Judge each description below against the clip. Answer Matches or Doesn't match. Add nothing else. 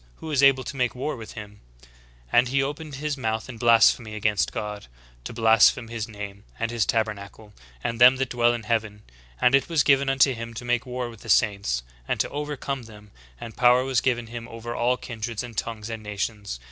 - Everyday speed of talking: Doesn't match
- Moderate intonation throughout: Matches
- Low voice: Matches